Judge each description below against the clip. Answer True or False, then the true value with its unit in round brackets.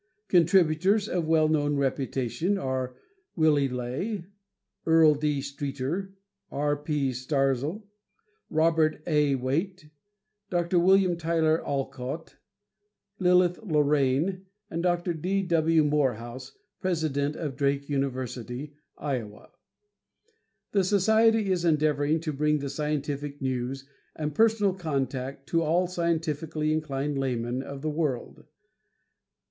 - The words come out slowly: True (110 wpm)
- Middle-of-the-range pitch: True (150 Hz)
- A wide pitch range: False (3.8 semitones)